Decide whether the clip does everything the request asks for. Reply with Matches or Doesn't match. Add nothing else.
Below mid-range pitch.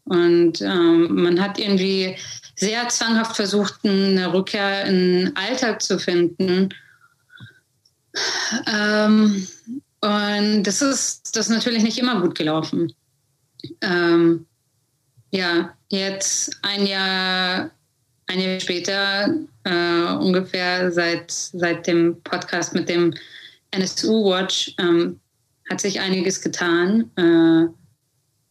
Doesn't match